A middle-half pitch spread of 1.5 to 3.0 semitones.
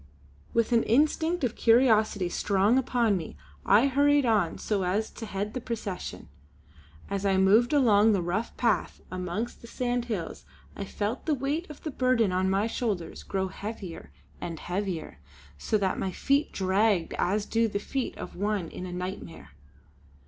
No: average, 4.2 semitones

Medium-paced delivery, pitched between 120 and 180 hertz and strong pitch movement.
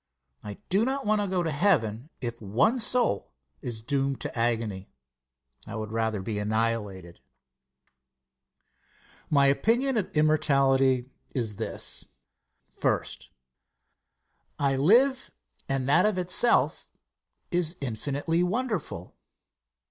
No: slow, 110 wpm; low, 135 Hz; wide, 8.5 semitones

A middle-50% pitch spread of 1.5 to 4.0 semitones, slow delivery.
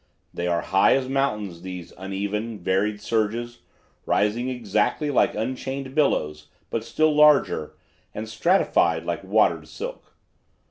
No: wide, 5.4 semitones; slow, 125 wpm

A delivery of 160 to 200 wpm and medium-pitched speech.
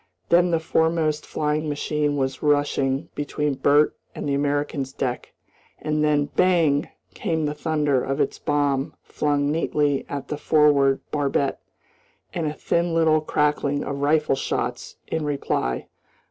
No: average, 140 wpm; medium, 145 Hz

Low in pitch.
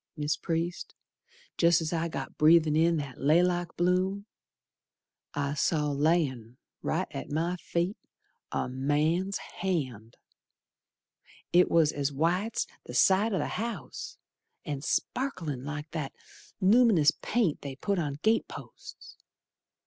No: medium, 165 Hz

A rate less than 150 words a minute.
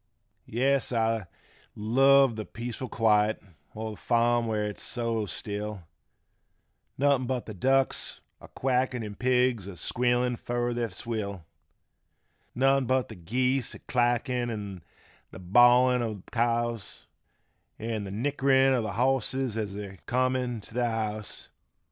Yes: slow, 135 wpm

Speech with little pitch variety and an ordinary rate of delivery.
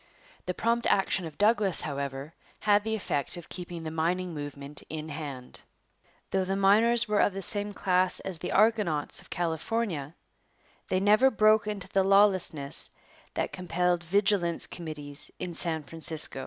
No: average, 4.4 semitones; average, 155 wpm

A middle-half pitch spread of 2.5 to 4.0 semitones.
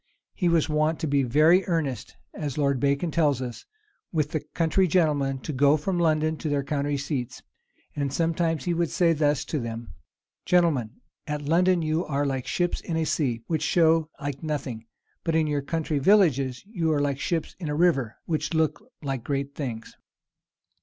Yes: average, 2.9 semitones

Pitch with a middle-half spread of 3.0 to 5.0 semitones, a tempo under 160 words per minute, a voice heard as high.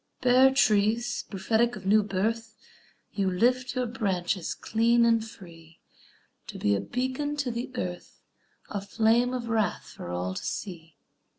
Yes: average, 4.4 semitones; average, 150 wpm; high, 220 Hz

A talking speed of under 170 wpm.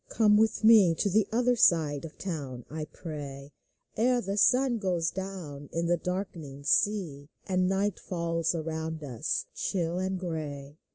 Yes: average, 160 wpm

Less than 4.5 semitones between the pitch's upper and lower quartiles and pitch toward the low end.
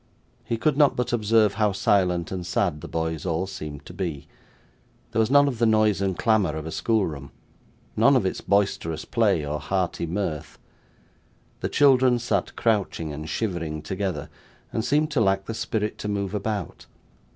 No: average, 5.2 semitones; low, 100 Hz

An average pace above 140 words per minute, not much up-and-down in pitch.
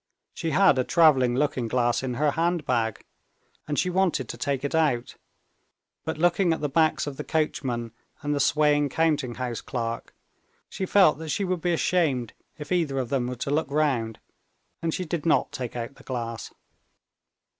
No: average, 180 wpm; average, 4.4 semitones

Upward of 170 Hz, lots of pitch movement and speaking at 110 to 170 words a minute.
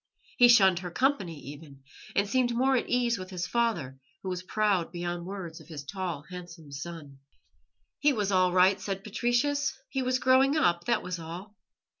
No: high, 190 Hz; wide, 5.8 semitones; average, 180 wpm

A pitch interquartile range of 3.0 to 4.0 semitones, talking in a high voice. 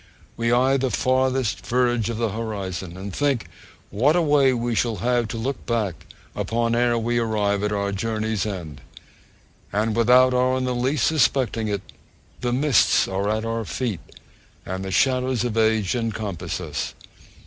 No: average, 3.3 semitones; low, 115 Hz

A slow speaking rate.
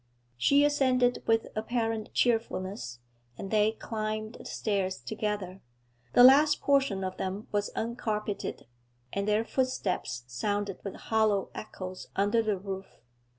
Yes: slow, 125 wpm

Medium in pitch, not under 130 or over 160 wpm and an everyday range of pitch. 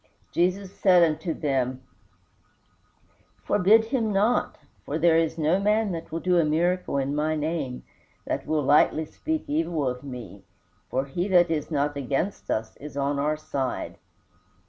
Yes: medium, 155 Hz; average, 155 wpm; average, 4.5 semitones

